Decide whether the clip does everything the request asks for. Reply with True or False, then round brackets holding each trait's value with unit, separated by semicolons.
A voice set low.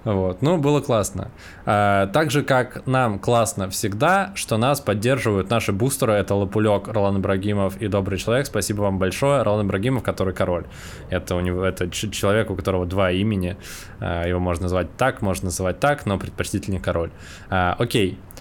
True (100 Hz)